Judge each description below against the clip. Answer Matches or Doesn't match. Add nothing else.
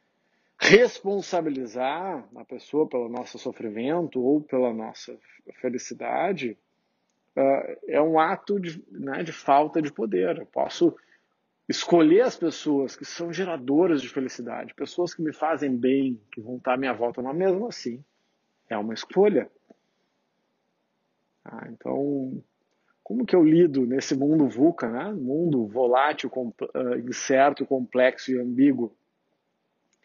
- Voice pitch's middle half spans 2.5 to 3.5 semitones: Doesn't match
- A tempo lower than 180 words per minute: Matches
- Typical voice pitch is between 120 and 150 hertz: Matches